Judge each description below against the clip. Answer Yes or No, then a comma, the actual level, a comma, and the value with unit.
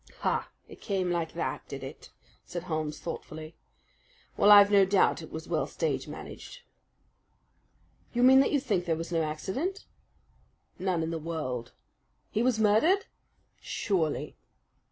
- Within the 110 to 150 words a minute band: Yes, average, 145 wpm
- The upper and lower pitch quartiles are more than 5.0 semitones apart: Yes, wide, 5.4 semitones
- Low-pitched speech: No, medium, 185 Hz